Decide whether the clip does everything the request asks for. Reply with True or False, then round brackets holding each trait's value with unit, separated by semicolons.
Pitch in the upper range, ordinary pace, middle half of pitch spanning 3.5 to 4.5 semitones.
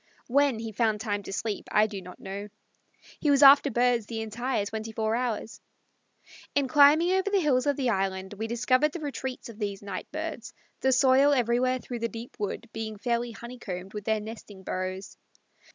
True (230 Hz; 185 wpm; 3.9 semitones)